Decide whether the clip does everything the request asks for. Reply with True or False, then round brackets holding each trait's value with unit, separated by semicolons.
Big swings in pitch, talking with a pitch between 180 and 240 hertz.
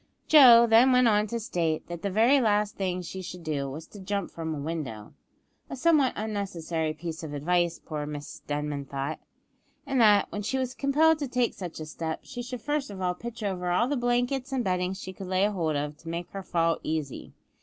True (6.8 semitones; 190 Hz)